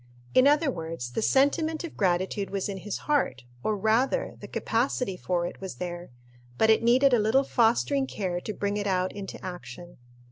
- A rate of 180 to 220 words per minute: Yes, average, 185 wpm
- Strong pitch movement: Yes, wide, 6.2 semitones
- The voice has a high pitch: Yes, high, 205 Hz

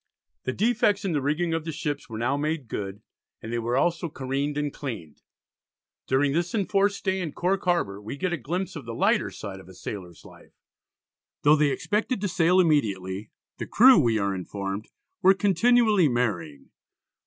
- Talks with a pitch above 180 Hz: No, medium, 145 Hz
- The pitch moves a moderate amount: No, wide, 8.5 semitones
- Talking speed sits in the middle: Yes, average, 180 wpm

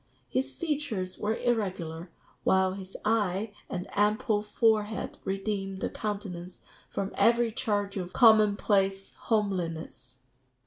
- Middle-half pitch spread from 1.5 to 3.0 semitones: Yes, narrow, 2.6 semitones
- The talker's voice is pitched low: No, high, 200 Hz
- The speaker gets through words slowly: Yes, slow, 115 wpm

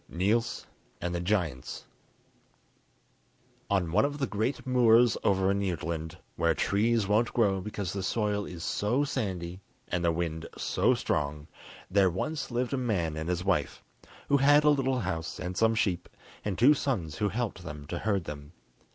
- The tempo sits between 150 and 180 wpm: Yes, average, 170 wpm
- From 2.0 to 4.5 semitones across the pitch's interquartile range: No, average, 5.3 semitones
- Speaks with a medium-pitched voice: No, low, 100 Hz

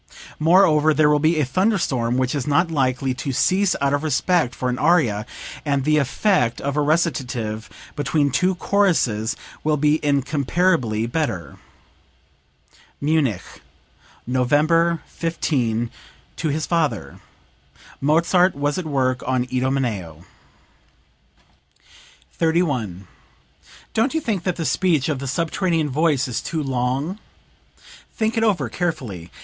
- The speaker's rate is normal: No, slow, 125 wpm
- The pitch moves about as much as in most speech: Yes, average, 4.7 semitones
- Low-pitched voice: No, medium, 145 Hz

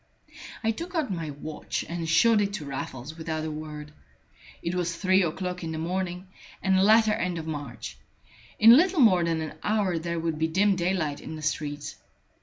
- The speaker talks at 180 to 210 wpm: Yes, average, 195 wpm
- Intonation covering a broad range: No, average, 3.6 semitones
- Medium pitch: Yes, medium, 170 Hz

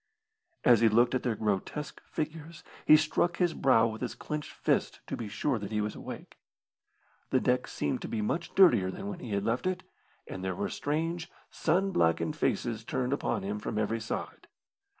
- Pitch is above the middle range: No, low, 120 Hz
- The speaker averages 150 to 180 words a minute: No, average, 190 wpm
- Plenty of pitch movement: Yes, wide, 6.6 semitones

